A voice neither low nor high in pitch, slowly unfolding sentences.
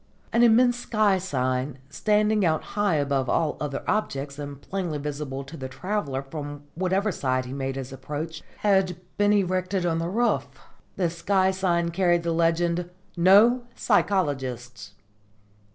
No: medium, 170 Hz; average, 145 wpm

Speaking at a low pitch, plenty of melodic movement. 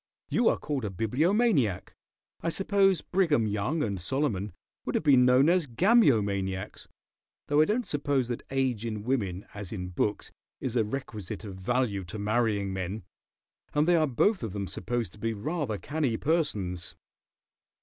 Yes: low, 120 Hz; wide, 6.7 semitones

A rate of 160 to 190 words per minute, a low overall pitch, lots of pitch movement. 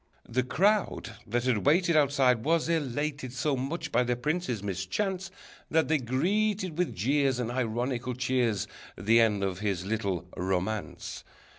No: average, 150 wpm; low, 130 Hz; wide, 5.9 semitones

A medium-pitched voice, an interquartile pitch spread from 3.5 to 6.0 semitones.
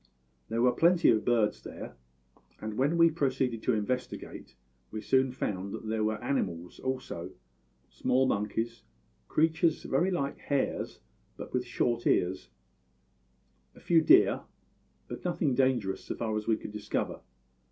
No: low, 125 Hz; average, 4.4 semitones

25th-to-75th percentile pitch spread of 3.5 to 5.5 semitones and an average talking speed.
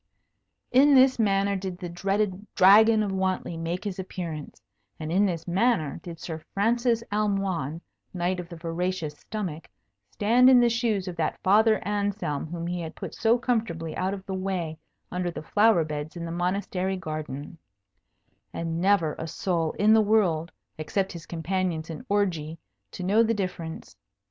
Yes: average, 3.8 semitones; average, 165 wpm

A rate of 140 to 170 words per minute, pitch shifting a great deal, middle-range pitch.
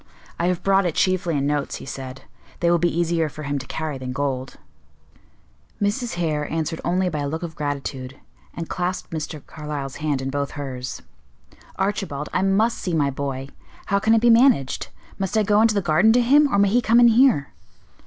No: fast, 205 wpm; wide, 5.8 semitones; medium, 165 Hz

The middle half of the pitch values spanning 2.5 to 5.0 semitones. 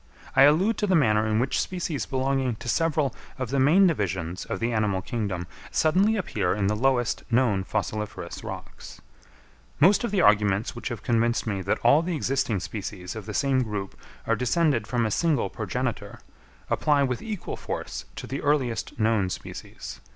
No: wide, 5.6 semitones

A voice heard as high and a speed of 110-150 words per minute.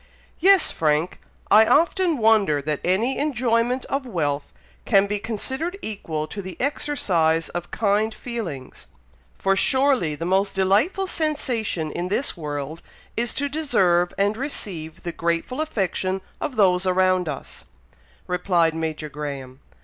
Yes: high, 195 Hz; slow, 135 wpm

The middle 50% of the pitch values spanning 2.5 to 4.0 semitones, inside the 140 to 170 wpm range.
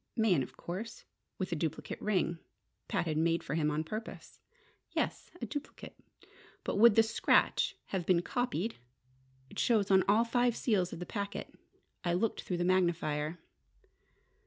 No: average, 4.7 semitones; average, 160 wpm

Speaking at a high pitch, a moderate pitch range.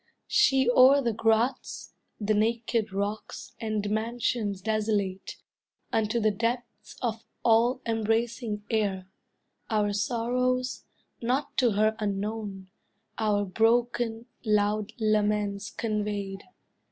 No: high, 220 Hz; narrow, 2.2 semitones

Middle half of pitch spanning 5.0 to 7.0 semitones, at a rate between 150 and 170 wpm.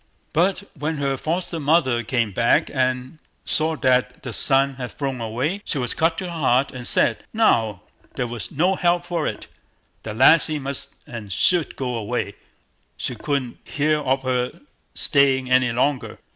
No: average, 4.0 semitones; average, 165 wpm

